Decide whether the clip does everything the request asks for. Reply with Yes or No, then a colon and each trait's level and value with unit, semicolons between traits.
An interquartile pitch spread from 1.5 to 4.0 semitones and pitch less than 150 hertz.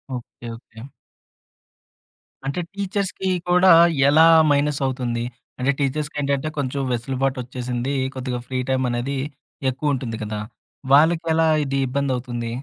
Yes: average, 2.9 semitones; low, 135 Hz